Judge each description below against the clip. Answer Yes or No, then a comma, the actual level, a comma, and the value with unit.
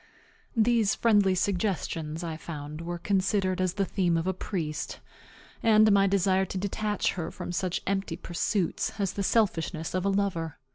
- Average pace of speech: Yes, average, 160 wpm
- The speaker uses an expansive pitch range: No, average, 2.8 semitones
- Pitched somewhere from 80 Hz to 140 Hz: No, high, 190 Hz